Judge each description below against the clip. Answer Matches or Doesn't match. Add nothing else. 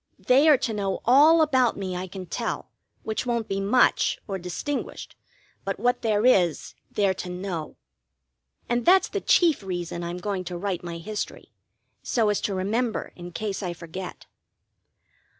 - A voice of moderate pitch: Doesn't match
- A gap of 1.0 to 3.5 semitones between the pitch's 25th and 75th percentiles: Doesn't match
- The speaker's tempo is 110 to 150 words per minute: Doesn't match